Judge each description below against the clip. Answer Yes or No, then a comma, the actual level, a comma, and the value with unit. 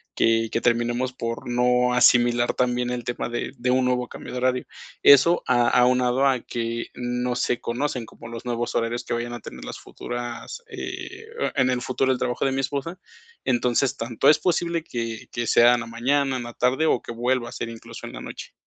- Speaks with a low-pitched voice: Yes, low, 125 Hz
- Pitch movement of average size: No, narrow, 1.4 semitones